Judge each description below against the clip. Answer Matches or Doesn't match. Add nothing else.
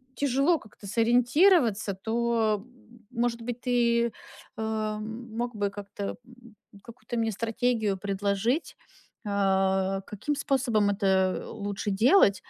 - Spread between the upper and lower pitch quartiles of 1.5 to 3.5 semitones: Matches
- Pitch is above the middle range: Matches